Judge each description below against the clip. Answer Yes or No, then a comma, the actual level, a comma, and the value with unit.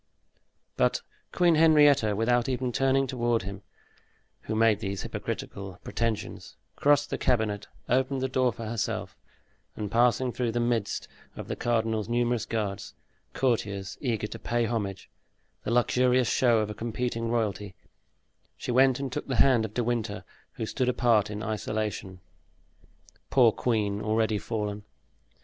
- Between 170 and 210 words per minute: No, average, 145 wpm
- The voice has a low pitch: Yes, low, 115 Hz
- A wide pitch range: No, average, 2.8 semitones